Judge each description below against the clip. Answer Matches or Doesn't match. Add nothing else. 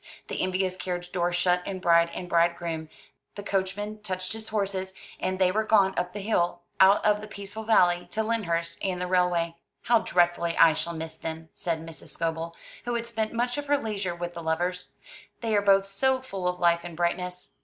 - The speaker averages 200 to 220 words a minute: Matches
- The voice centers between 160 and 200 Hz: Matches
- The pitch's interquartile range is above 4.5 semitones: Doesn't match